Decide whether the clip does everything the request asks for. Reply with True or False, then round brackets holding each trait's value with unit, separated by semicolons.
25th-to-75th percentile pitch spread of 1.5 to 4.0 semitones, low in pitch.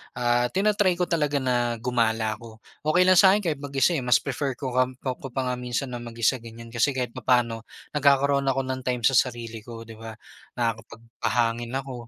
True (2.9 semitones; 125 Hz)